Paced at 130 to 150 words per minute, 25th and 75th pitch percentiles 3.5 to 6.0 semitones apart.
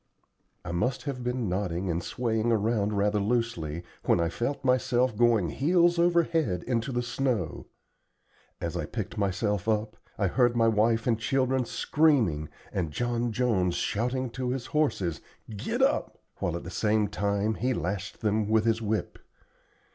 No: average, 160 wpm; average, 3.8 semitones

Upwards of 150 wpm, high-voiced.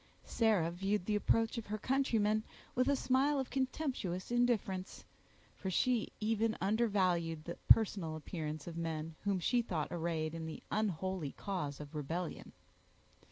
No: average, 145 wpm; high, 195 Hz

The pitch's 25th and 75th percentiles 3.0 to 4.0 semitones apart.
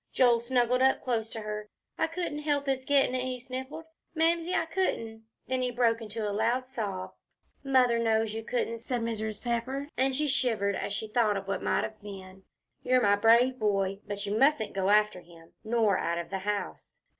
Yes: average, 3.7 semitones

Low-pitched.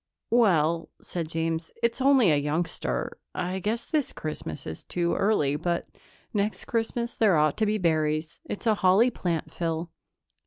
No: medium, 175 Hz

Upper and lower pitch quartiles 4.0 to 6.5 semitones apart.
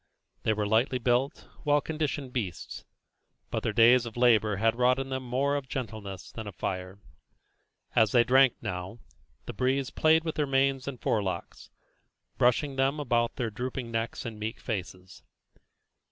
No: average, 3.5 semitones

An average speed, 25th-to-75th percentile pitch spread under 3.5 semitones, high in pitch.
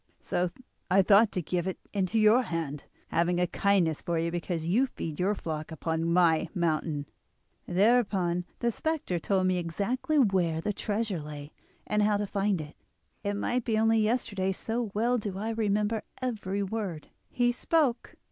No: average, 165 wpm; average, 4.5 semitones; high, 195 Hz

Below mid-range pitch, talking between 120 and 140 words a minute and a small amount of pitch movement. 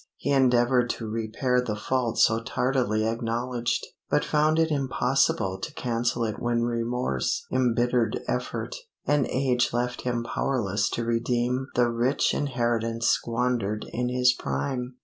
Yes: low, 120 Hz; slow, 135 wpm; narrow, 1.7 semitones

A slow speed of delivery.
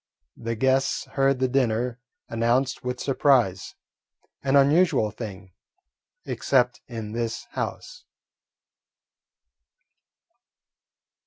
Yes: slow, 80 wpm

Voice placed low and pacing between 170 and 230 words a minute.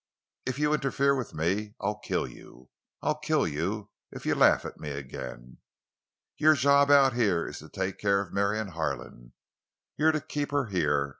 Yes: low, 105 Hz; average, 175 wpm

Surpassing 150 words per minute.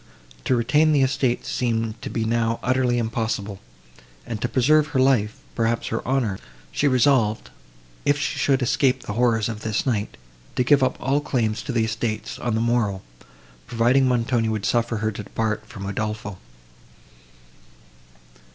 Yes: average, 160 wpm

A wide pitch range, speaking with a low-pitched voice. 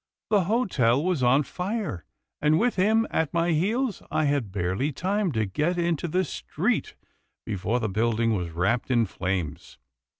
No: wide, 8.8 semitones; medium, 145 Hz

